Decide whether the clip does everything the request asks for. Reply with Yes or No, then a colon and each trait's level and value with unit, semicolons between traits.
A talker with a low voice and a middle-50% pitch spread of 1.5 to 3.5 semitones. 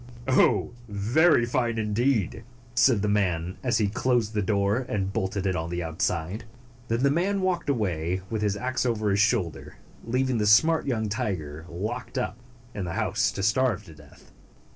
No: low, 105 Hz; average, 4.6 semitones